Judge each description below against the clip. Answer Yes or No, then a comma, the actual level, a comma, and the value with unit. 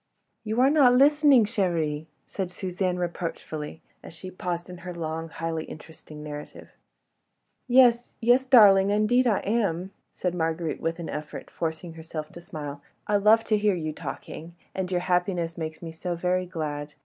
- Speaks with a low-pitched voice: No, medium, 180 Hz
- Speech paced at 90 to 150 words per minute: No, average, 160 wpm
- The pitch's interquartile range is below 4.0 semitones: No, average, 4.3 semitones